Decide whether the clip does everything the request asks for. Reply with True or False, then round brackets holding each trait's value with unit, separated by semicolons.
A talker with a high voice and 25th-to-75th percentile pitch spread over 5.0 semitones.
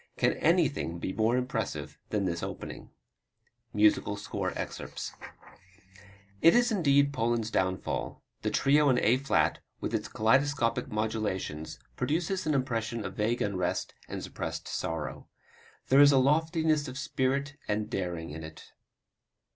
False (120 Hz; 5.6 semitones)